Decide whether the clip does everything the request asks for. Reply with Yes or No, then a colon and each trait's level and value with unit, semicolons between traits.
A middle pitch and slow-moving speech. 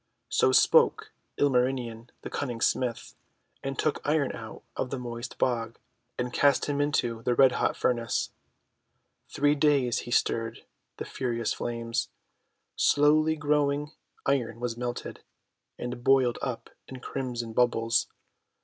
No: low, 125 Hz; slow, 130 wpm